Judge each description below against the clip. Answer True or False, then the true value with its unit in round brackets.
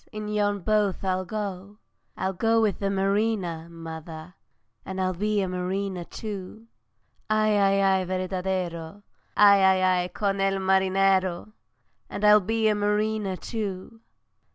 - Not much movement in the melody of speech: True (2.1 semitones)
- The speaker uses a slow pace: True (130 wpm)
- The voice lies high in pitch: True (195 Hz)